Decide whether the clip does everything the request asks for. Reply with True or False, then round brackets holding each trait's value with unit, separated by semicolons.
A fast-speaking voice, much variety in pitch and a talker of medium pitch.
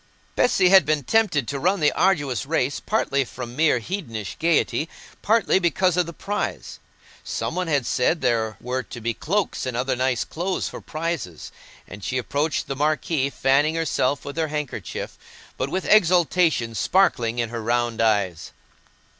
False (165 wpm; 6.0 semitones; 145 Hz)